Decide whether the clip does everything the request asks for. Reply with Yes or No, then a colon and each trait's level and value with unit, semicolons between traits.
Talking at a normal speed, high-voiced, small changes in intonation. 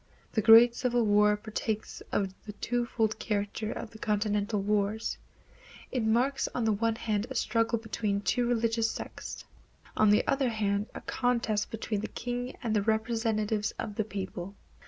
Yes: average, 155 wpm; high, 220 Hz; narrow, 1.9 semitones